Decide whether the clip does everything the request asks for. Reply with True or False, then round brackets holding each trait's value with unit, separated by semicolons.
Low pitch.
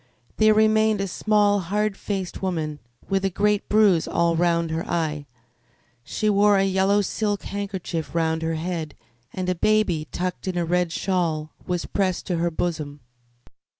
False (185 Hz)